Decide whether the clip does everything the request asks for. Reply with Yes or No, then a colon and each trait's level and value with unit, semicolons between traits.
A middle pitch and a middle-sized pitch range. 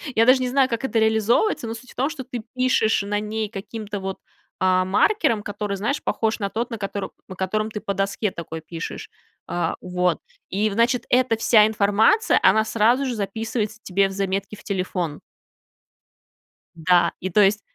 No: high, 210 Hz; average, 3.0 semitones